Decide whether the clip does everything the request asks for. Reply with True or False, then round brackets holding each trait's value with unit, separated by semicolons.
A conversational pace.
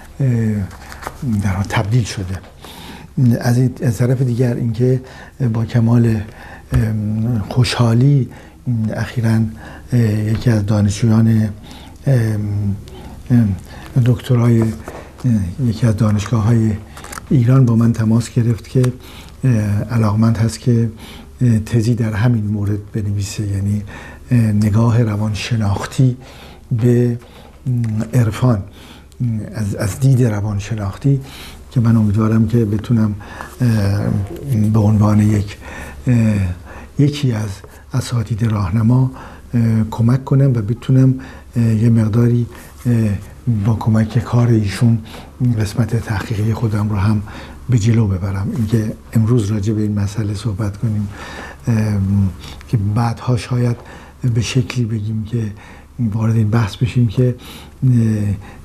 False (95 wpm)